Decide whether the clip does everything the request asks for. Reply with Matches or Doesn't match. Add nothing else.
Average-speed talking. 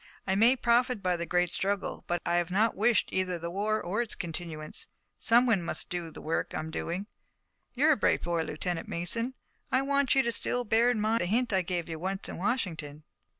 Doesn't match